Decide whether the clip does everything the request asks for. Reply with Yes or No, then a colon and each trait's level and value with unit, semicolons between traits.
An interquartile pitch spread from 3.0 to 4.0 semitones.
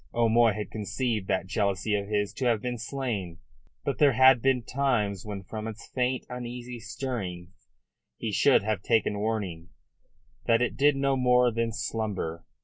Yes: average, 3.4 semitones